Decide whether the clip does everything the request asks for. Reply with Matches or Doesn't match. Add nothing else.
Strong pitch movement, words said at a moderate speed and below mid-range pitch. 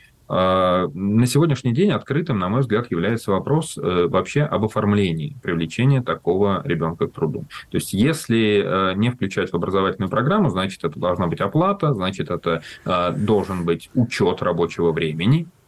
Matches